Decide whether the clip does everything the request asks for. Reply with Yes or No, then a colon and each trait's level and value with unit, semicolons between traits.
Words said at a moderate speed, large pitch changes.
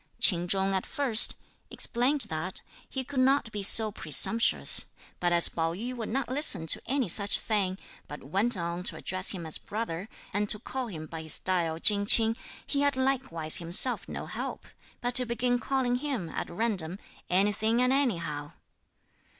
Yes: average, 175 wpm; wide, 6.2 semitones